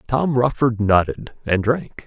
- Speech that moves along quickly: No, average, 145 wpm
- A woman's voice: No, male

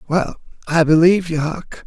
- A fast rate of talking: No, average, 160 wpm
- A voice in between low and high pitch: Yes, medium, 165 Hz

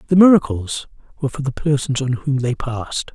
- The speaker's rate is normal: Yes, average, 190 wpm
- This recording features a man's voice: Yes, male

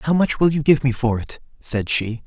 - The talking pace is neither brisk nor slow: No, fast, 265 wpm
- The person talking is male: Yes, male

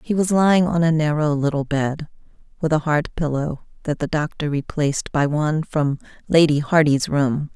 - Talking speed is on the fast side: No, average, 175 wpm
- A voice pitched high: No, medium, 150 Hz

